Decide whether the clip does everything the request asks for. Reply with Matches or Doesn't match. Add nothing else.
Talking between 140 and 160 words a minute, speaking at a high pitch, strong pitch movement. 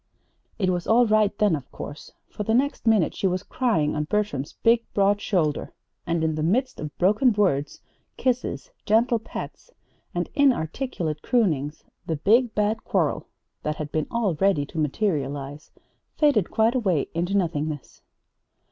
Matches